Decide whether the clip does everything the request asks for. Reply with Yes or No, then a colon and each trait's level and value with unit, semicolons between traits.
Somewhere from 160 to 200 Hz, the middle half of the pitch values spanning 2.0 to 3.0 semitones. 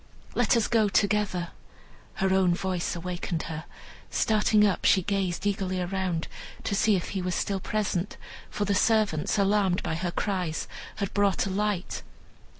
Yes: high, 190 Hz; narrow, 2.4 semitones